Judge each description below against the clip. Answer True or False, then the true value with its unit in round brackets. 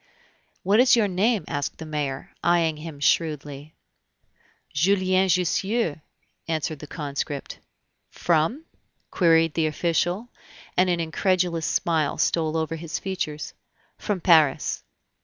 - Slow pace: True (120 wpm)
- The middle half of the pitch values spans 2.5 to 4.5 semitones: True (3.3 semitones)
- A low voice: False (165 Hz)